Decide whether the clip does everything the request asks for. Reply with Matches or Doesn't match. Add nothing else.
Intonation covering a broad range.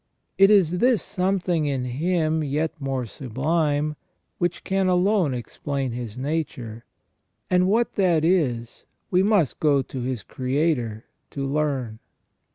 Matches